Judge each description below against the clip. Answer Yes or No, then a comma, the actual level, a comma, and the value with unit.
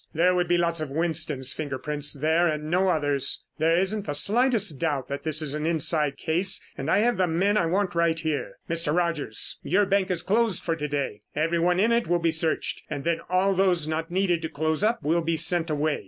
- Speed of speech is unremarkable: No, fast, 225 wpm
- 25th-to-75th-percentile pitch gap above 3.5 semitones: No, average, 3.0 semitones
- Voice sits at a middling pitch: Yes, medium, 165 Hz